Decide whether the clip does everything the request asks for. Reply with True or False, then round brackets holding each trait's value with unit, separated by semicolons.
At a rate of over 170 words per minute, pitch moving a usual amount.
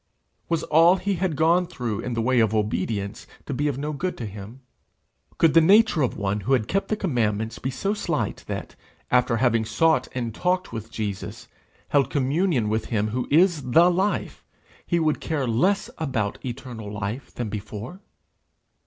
False (180 wpm; 6.9 semitones)